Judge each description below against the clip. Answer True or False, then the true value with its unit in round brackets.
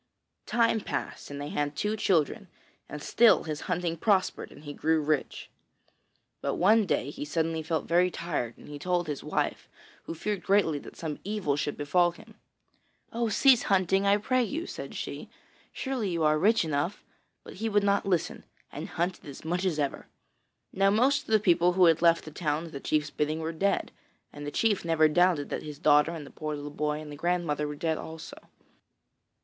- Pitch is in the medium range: True (170 Hz)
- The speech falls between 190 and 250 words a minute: True (200 wpm)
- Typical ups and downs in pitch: True (4.7 semitones)